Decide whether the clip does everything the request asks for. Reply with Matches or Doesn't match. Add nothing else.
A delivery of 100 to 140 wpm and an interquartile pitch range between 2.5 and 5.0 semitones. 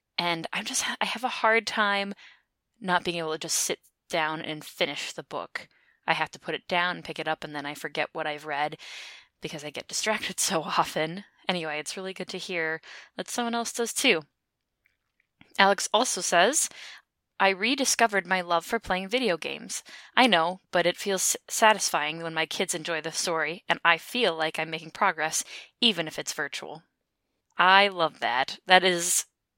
Doesn't match